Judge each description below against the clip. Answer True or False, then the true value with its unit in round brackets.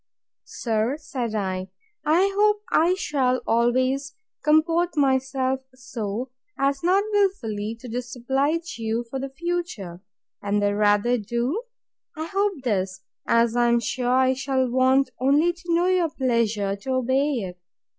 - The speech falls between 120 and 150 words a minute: True (140 wpm)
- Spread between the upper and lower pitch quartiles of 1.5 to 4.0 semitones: False (5.1 semitones)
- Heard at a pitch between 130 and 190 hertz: False (260 Hz)